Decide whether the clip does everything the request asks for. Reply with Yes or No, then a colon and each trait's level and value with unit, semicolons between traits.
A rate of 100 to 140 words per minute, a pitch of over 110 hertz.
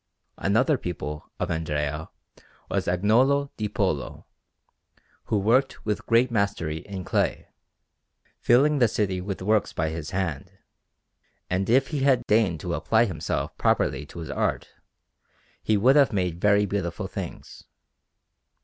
No: slow, 135 wpm; low, 100 Hz